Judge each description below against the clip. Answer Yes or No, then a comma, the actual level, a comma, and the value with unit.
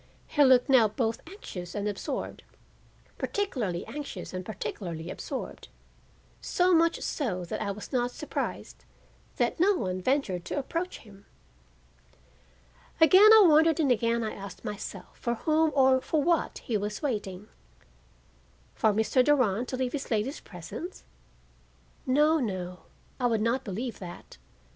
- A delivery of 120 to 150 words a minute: Yes, average, 140 wpm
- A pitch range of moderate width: No, wide, 6.7 semitones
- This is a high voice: Yes, high, 240 Hz